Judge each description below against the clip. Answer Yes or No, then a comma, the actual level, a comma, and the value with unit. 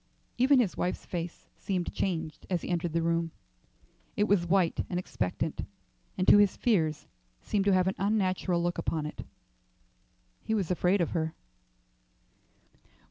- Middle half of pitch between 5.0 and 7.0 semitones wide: No, average, 2.8 semitones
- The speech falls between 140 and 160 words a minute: Yes, average, 150 wpm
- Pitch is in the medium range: Yes, medium, 180 Hz